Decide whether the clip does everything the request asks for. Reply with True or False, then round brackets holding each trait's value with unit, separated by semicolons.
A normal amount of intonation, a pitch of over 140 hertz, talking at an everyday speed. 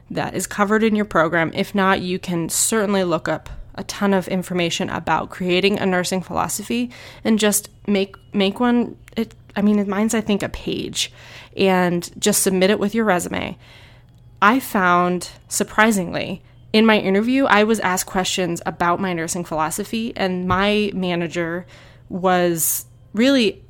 True (3.1 semitones; 190 Hz; 155 wpm)